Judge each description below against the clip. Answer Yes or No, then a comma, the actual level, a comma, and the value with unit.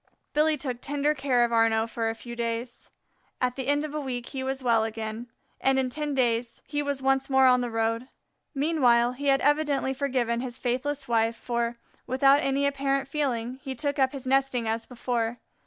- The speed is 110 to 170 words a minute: No, average, 195 wpm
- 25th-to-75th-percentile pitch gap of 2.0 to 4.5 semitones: Yes, average, 2.8 semitones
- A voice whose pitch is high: Yes, very high, 260 Hz